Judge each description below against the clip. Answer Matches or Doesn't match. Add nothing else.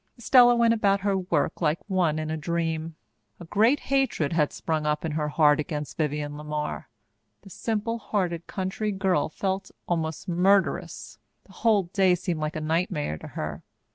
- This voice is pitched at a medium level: Matches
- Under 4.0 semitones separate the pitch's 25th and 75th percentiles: Doesn't match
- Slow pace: Doesn't match